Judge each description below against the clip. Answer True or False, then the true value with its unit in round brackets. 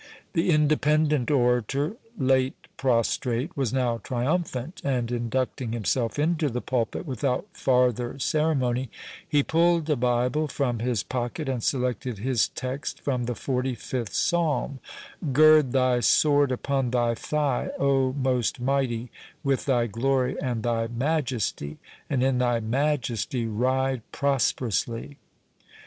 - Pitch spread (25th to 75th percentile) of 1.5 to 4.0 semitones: True (2.8 semitones)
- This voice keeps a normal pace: False (125 wpm)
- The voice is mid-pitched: False (130 Hz)